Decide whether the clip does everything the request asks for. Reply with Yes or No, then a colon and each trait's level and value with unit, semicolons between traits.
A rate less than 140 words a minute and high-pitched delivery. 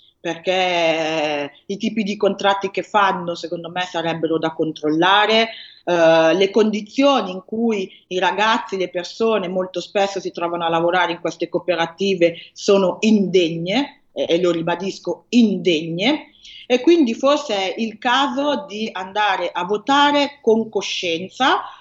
Yes: average, 130 wpm; high, 195 Hz